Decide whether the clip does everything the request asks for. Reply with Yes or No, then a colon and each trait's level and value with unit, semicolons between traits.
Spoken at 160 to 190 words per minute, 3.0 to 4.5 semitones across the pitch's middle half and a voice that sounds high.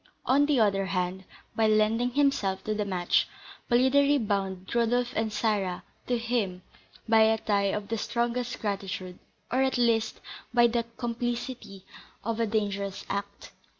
No: average, 150 wpm; average, 3.3 semitones; high, 220 Hz